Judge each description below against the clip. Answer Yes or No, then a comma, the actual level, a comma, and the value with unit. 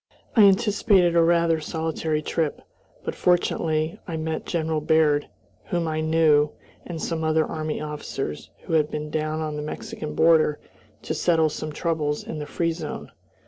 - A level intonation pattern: Yes, narrow, 1.5 semitones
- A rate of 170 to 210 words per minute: No, average, 160 wpm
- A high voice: No, medium, 160 Hz